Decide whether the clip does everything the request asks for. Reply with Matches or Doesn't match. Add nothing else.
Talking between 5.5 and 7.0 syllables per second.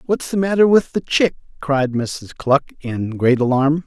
Doesn't match